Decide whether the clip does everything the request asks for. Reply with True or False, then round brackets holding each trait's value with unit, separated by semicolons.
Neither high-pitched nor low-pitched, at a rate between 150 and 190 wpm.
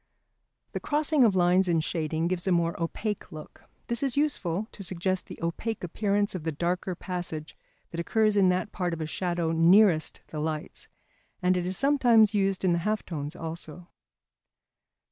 True (180 Hz; 175 wpm)